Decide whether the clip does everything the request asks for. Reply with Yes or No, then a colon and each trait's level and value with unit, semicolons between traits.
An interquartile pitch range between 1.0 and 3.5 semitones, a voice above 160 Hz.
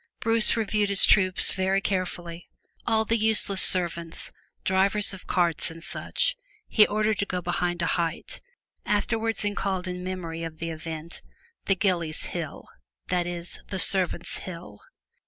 Yes: average, 3.1 semitones; medium, 185 Hz